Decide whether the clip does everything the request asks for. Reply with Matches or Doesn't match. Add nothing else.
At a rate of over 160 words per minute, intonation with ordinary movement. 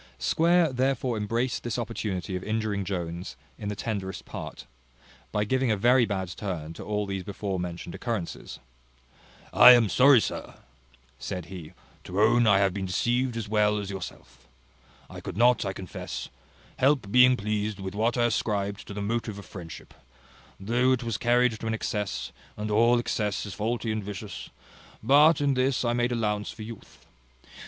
Matches